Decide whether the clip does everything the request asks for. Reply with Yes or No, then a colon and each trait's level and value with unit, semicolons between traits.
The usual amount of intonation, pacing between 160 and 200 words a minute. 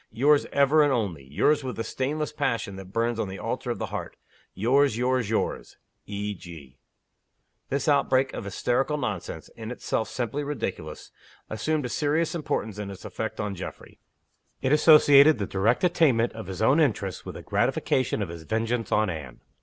No: wide, 5.9 semitones; average, 175 wpm